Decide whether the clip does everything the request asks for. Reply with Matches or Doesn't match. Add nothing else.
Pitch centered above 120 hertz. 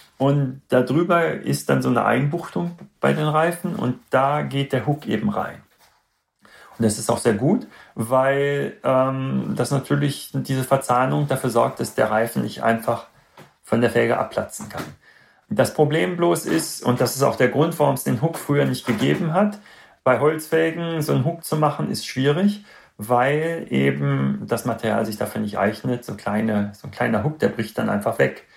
Matches